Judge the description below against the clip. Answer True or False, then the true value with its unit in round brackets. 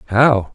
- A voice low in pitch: True (115 Hz)